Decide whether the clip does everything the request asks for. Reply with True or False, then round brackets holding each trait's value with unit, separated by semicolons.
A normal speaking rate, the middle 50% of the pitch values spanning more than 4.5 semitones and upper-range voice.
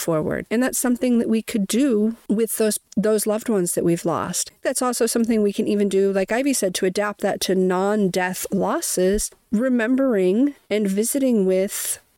False (175 wpm; 3.4 semitones; 215 Hz)